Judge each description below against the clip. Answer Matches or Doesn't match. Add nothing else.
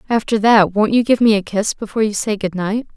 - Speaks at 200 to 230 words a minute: Doesn't match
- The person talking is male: Doesn't match